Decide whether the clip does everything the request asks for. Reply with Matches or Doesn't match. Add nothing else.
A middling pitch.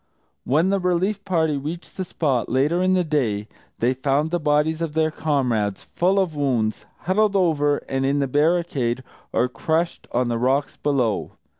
Matches